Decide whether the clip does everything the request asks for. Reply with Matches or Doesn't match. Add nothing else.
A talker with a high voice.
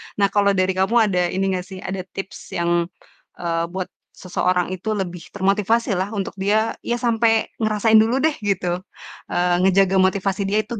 Matches